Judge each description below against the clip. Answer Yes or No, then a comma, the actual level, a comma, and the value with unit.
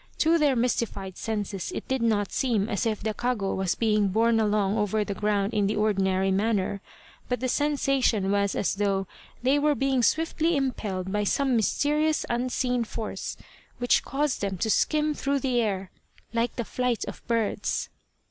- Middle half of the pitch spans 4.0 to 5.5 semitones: Yes, average, 4.3 semitones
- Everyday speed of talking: Yes, average, 170 wpm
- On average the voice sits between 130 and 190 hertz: No, high, 225 Hz